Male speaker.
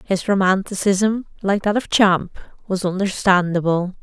No: female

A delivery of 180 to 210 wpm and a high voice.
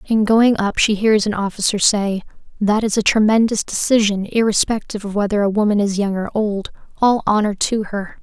Yes: average, 190 wpm; high, 210 Hz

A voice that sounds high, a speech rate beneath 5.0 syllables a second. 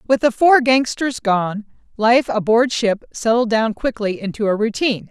Yes: high, 230 Hz; 4.7 syllables/s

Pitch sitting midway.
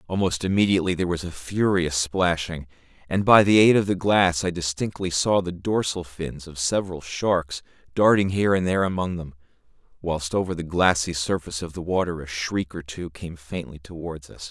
No: very low, 85 Hz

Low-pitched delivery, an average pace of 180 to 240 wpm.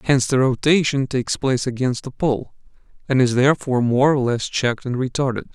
Yes: low, 130 Hz; average, 185 wpm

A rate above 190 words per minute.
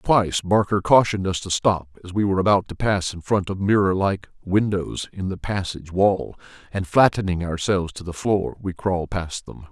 Yes: average, 200 wpm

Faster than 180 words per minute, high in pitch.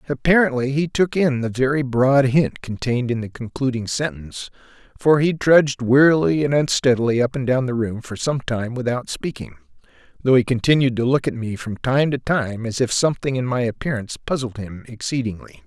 No: average, 190 wpm; low, 125 Hz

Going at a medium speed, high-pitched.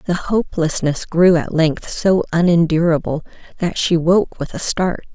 No: average, 150 wpm; medium, 170 Hz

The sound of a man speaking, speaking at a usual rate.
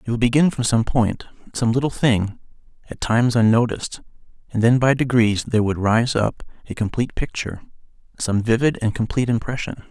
Yes: male; average, 170 wpm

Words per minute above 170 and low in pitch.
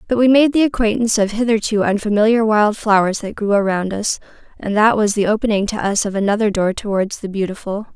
No: fast, 205 wpm; high, 210 Hz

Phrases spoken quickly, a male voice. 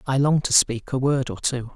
Yes: fast, 275 wpm; male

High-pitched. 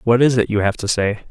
No: low, 110 Hz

